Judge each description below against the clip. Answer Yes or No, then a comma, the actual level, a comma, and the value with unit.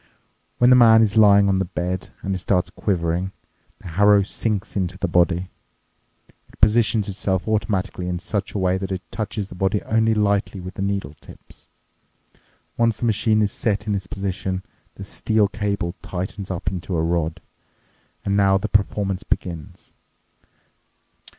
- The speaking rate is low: No, average, 165 wpm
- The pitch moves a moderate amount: No, narrow, 2.2 semitones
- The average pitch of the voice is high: No, low, 100 Hz